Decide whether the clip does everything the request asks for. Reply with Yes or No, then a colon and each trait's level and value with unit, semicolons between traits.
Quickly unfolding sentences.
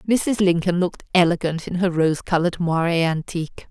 No: average, 160 wpm